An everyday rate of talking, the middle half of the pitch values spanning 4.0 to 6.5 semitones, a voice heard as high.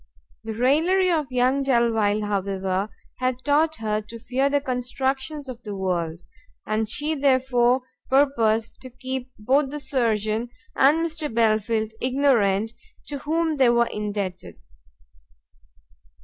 No: slow, 125 wpm; average, 4.4 semitones; very high, 250 Hz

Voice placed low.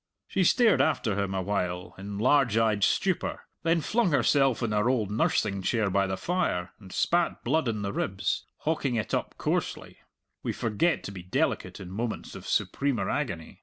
Yes: low, 110 Hz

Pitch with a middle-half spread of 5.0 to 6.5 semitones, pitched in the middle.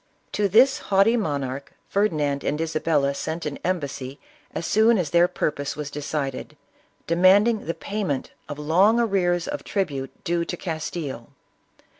Yes: wide, 5.5 semitones; medium, 165 Hz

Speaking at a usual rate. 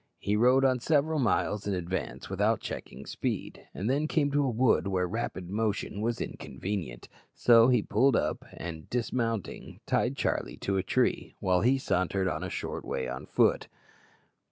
Yes: average, 170 wpm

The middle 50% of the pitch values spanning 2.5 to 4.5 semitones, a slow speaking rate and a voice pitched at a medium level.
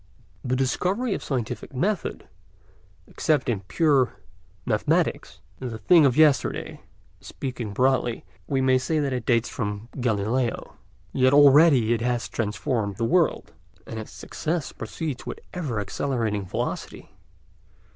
No: average, 4.2 semitones; slow, 130 wpm; low, 130 Hz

